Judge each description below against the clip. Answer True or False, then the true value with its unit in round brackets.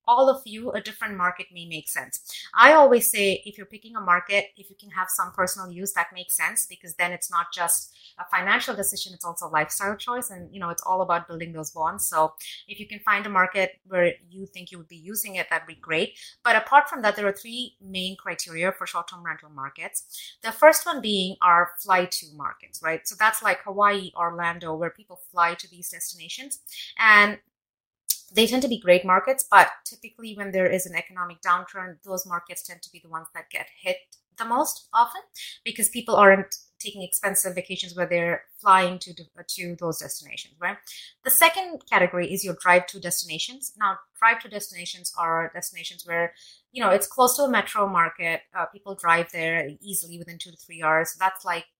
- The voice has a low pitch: False (185 Hz)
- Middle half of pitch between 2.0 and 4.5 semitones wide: True (3.2 semitones)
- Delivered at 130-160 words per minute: False (205 wpm)